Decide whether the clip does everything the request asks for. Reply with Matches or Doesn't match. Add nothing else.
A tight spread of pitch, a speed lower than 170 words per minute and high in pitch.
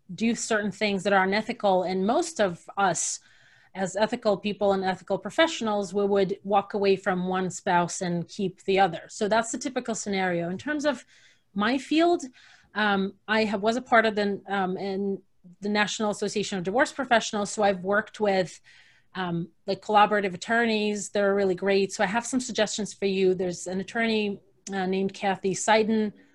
Doesn't match